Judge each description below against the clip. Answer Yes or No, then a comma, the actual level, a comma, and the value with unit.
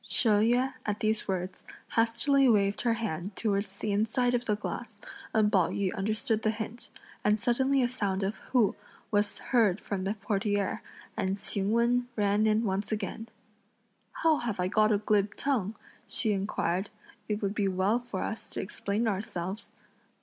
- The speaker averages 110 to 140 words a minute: No, average, 170 wpm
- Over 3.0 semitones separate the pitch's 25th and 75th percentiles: No, narrow, 2.5 semitones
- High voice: Yes, high, 210 Hz